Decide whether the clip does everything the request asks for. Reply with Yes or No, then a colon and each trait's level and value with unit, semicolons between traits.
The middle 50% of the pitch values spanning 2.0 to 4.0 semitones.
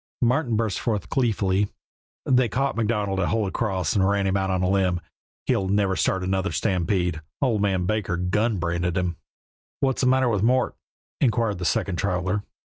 Yes: average, 3.6 semitones